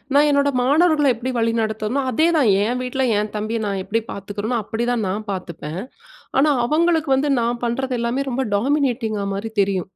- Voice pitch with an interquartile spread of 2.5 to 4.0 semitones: No, average, 4.5 semitones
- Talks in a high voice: Yes, high, 235 Hz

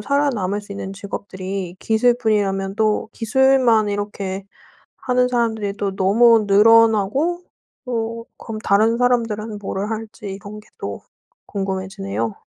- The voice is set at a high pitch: Yes, high, 210 Hz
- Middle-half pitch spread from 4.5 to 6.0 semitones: No, average, 2.8 semitones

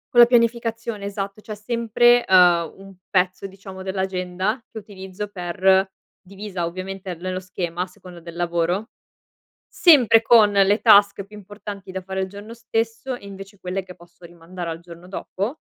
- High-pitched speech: Yes, high, 195 Hz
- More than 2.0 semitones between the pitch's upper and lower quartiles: Yes, average, 2.7 semitones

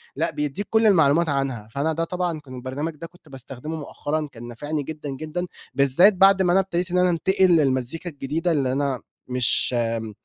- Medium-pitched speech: Yes, medium, 155 Hz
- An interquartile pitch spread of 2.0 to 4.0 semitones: No, average, 4.4 semitones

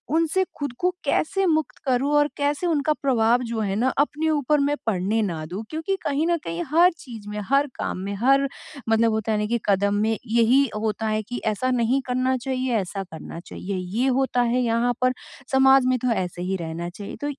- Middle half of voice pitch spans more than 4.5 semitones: Yes, average, 4.9 semitones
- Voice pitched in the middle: No, high, 245 Hz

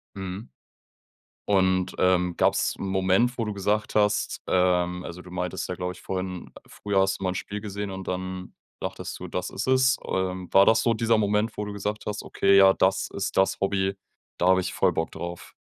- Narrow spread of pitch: Yes, narrow, 2.0 semitones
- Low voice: Yes, very low, 95 Hz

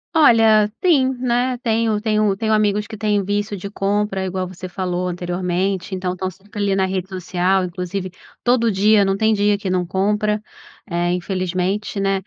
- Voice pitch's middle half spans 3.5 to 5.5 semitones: No, narrow, 2.4 semitones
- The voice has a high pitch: Yes, high, 195 Hz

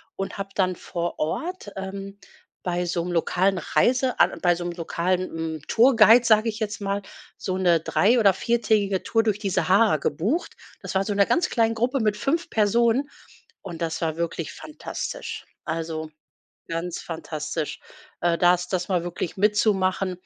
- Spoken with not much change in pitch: No, average, 4.1 semitones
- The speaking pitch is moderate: No, high, 195 Hz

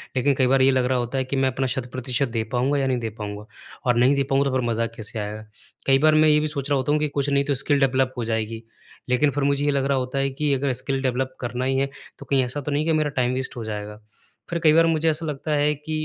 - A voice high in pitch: No, low, 135 Hz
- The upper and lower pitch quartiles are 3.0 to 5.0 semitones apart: No, narrow, 2.5 semitones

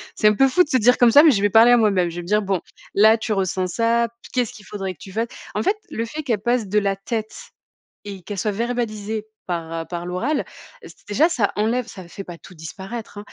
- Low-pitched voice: No, high, 210 Hz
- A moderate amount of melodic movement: Yes, average, 3.5 semitones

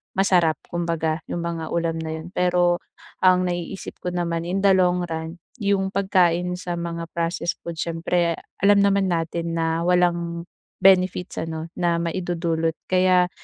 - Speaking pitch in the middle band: Yes, medium, 175 Hz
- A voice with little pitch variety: Yes, narrow, 1.5 semitones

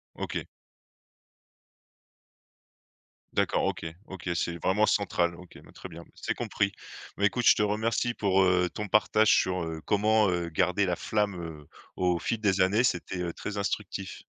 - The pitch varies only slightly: No, average, 3.1 semitones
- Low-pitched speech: Yes, very low, 95 Hz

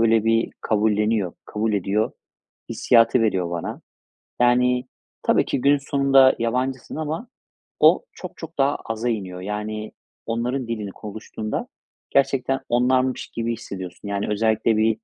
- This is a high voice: No, low, 115 Hz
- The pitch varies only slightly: No, average, 3.2 semitones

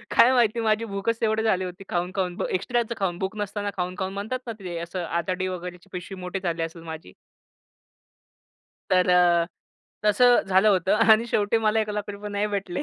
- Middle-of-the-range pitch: No, high, 195 Hz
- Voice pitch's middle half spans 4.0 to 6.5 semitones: No, average, 3.1 semitones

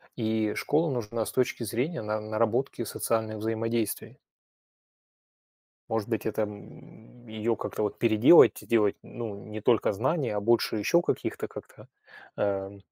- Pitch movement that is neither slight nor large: No, narrow, 1.9 semitones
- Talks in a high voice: No, low, 110 Hz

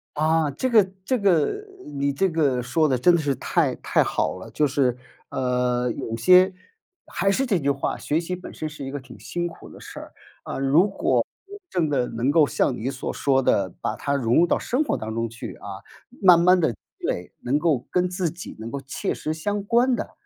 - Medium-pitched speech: Yes, medium, 145 Hz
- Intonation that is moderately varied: No, wide, 6.0 semitones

